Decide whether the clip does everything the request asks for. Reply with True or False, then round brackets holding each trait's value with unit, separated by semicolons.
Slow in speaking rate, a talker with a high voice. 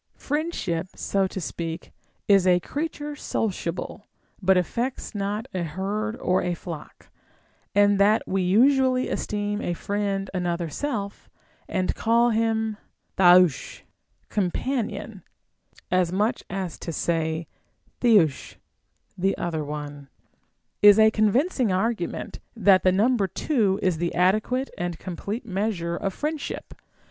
True (125 wpm; 195 Hz)